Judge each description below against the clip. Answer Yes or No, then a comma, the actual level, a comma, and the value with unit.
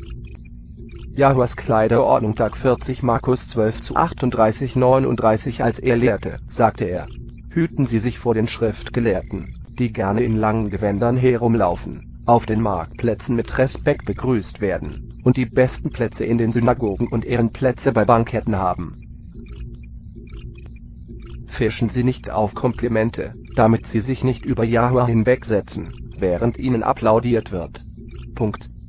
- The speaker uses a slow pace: Yes, slow, 130 wpm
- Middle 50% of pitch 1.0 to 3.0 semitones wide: Yes, average, 2.7 semitones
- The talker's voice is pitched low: Yes, low, 115 Hz